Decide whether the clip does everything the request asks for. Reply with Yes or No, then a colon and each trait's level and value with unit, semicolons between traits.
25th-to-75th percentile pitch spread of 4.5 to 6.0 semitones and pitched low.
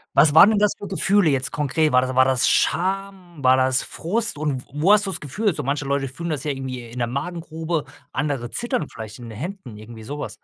No: wide, 5.4 semitones; medium, 145 Hz